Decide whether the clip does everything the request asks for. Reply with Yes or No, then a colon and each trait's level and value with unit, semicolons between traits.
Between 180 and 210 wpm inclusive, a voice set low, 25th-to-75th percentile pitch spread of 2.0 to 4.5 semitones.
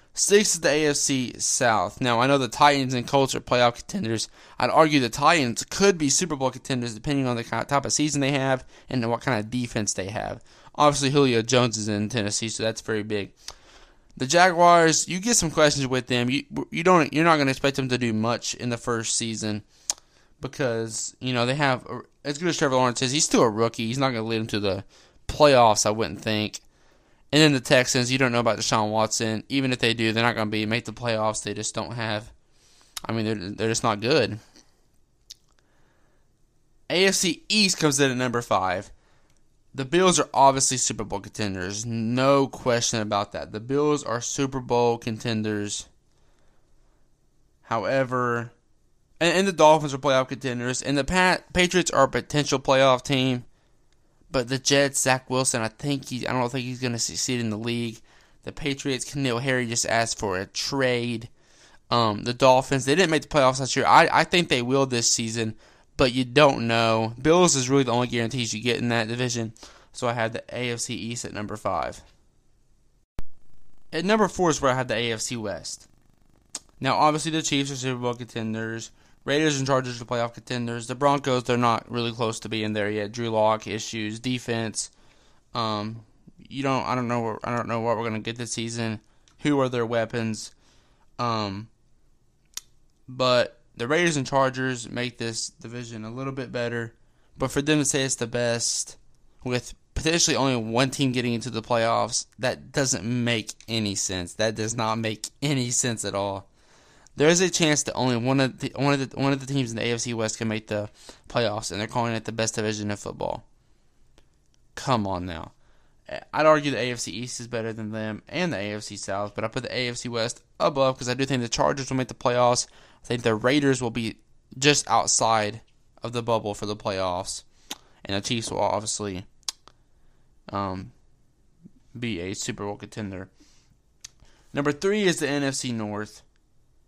Yes: average, 190 wpm; low, 120 Hz; average, 3.4 semitones